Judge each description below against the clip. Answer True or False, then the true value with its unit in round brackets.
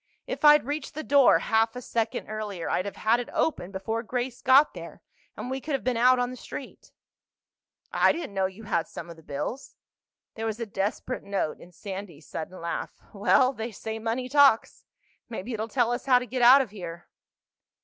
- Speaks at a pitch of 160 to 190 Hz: False (225 Hz)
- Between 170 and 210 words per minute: True (200 wpm)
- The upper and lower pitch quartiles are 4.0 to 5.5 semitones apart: True (4.3 semitones)